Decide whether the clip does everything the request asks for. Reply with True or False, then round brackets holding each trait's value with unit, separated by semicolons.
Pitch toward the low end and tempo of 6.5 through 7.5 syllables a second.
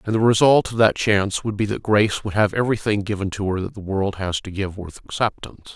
False (105 Hz; 6.1 syllables/s)